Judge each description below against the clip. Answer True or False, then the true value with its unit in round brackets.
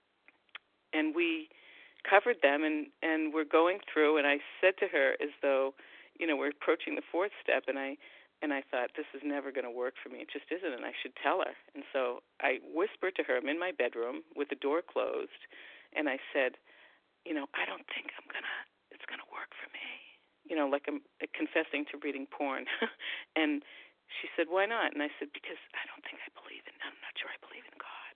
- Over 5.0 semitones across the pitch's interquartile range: True (5.6 semitones)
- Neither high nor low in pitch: True (150 Hz)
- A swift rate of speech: True (215 wpm)